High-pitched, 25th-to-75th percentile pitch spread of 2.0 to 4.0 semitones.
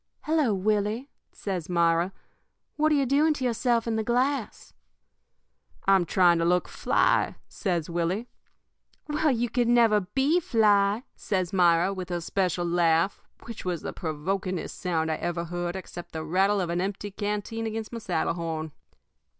No: high, 195 Hz; average, 4.8 semitones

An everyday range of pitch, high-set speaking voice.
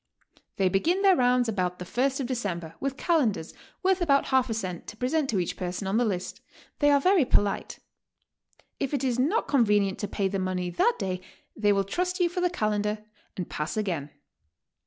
No: wide, 6.6 semitones; high, 220 Hz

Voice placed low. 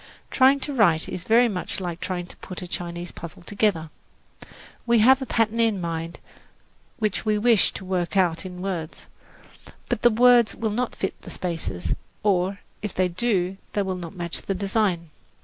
No: high, 190 Hz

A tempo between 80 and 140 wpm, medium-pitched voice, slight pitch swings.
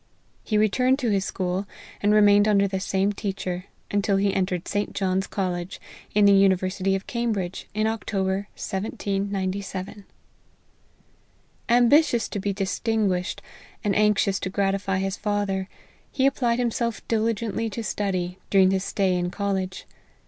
No: slow, 135 wpm; high, 200 Hz; narrow, 1.9 semitones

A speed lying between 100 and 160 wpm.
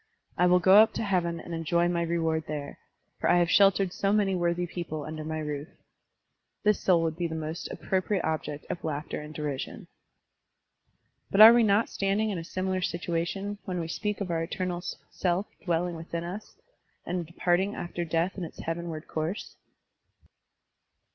No: average, 180 wpm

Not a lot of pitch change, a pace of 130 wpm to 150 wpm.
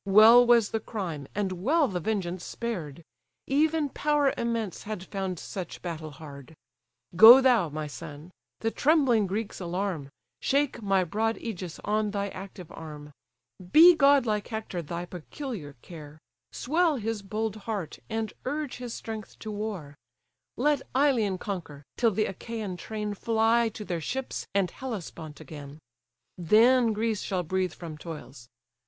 No: average, 5.1 semitones; average, 145 wpm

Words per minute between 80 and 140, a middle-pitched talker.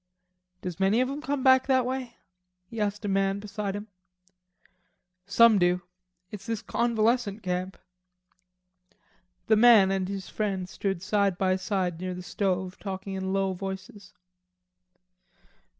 No: slow, 135 wpm; high, 195 Hz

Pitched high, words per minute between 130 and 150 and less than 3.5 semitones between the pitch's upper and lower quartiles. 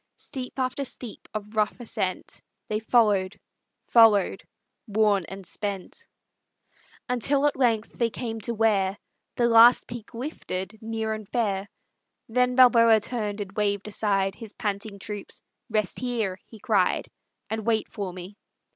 Yes: high, 220 Hz; average, 140 wpm; narrow, 2.6 semitones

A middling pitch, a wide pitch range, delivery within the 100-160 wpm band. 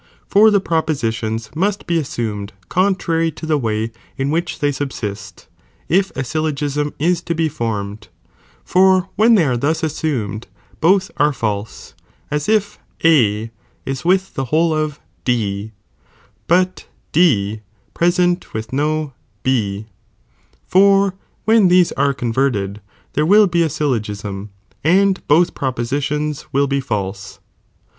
Yes: medium, 145 Hz; wide, 7.4 semitones; slow, 135 wpm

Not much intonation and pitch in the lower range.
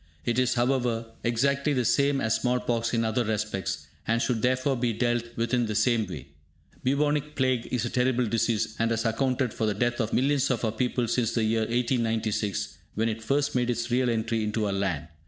Yes: narrow, 2.2 semitones; low, 120 Hz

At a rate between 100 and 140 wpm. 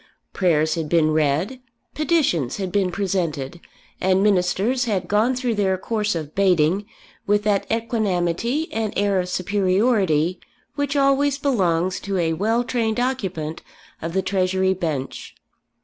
Yes: slow, 135 wpm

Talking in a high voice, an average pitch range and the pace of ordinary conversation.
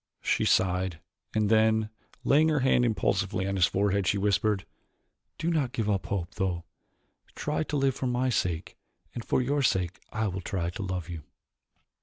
No: low, 105 Hz; average, 4.9 semitones; average, 175 wpm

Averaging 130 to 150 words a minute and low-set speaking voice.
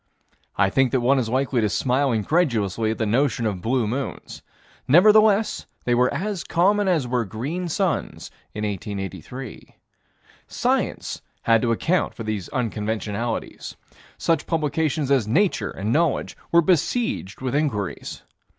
Yes: average, 140 wpm; low, 125 Hz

